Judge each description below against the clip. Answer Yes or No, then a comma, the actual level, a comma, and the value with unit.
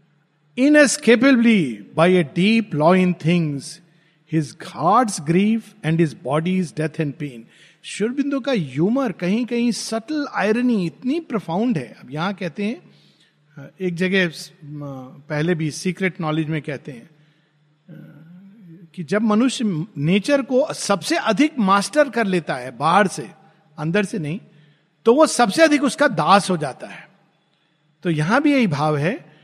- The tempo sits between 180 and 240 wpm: No, average, 135 wpm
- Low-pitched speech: No, medium, 180 Hz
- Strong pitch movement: Yes, wide, 5.8 semitones